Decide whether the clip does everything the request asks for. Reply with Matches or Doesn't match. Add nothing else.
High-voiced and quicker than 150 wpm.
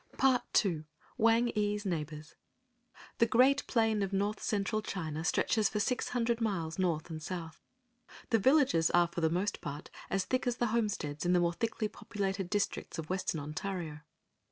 Matches